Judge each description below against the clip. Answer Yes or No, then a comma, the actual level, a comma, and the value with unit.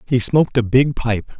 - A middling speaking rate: No, fast, 215 wpm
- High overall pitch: No, low, 125 Hz